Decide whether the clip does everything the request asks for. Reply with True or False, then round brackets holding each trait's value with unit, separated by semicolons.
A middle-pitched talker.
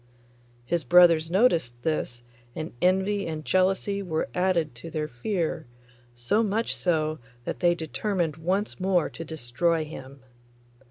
True (165 Hz)